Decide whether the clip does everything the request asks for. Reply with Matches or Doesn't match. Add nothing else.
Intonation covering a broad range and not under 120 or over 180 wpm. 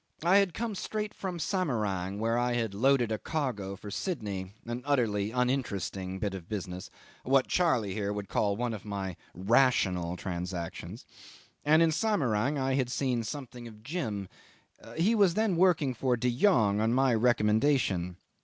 Matches